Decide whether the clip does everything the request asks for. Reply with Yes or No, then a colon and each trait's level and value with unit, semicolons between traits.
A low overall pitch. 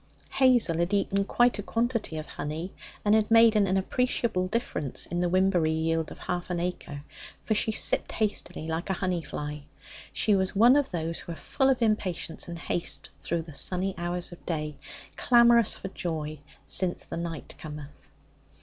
No: medium, 180 Hz